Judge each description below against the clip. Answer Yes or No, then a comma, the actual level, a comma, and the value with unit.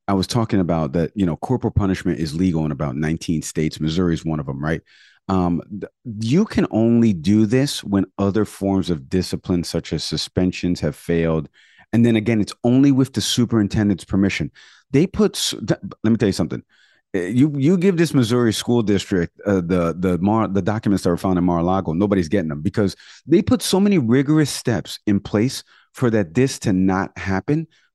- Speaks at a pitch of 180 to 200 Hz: No, low, 100 Hz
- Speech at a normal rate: Yes, average, 190 wpm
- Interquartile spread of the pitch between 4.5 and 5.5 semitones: Yes, average, 5.1 semitones